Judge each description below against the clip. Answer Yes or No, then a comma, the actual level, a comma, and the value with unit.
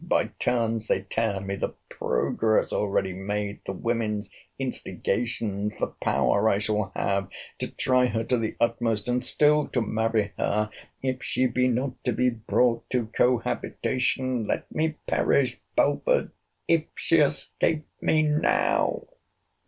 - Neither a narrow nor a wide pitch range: Yes, average, 3.3 semitones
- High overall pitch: No, low, 115 Hz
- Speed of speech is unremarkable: No, slow, 130 wpm